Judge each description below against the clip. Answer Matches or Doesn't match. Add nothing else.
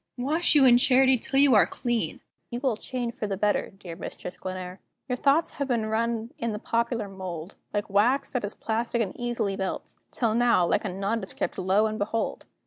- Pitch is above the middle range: Matches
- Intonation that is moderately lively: Matches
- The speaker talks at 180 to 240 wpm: Matches